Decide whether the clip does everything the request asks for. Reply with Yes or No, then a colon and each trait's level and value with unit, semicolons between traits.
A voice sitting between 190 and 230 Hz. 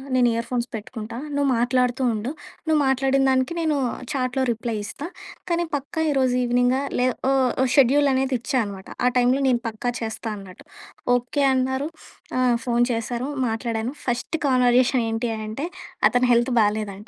No: very high, 250 Hz